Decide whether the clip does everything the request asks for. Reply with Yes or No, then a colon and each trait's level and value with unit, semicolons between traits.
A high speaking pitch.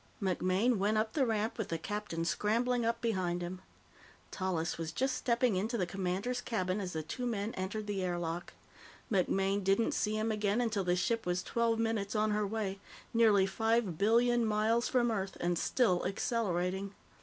Yes: high, 210 Hz